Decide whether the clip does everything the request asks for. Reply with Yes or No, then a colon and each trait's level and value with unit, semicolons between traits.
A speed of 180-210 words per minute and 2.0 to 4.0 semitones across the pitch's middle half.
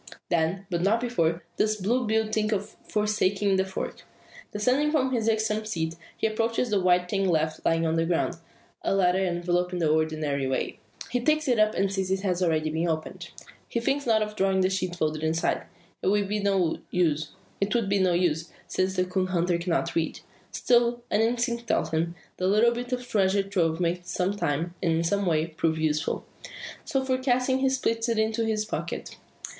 No: average, 190 wpm; average, 4.6 semitones